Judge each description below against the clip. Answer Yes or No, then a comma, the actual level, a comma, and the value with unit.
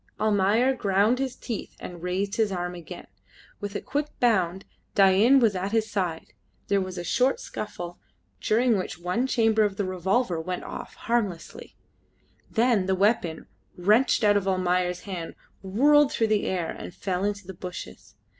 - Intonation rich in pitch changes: No, average, 3.6 semitones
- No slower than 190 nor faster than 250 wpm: No, average, 165 wpm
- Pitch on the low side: No, high, 200 Hz